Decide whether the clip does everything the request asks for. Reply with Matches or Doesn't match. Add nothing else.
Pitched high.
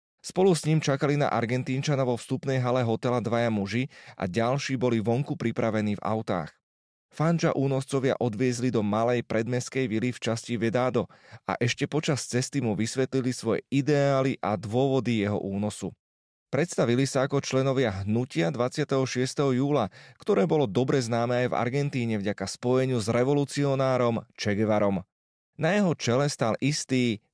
Doesn't match